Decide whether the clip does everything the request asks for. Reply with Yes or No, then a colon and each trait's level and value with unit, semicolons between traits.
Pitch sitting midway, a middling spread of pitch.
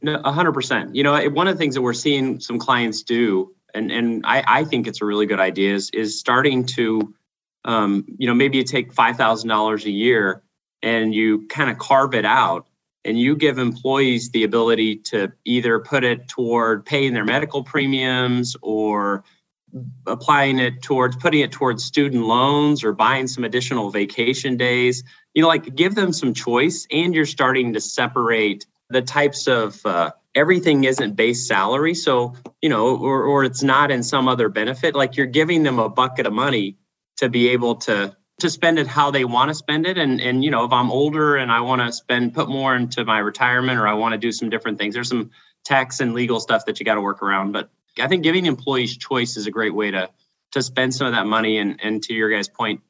No: low, 125 Hz; average, 3.6 semitones